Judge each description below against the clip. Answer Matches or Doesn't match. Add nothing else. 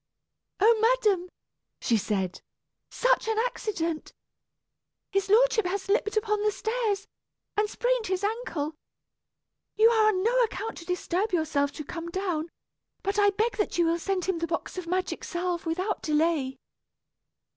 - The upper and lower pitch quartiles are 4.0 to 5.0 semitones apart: Matches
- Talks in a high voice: Matches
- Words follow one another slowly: Doesn't match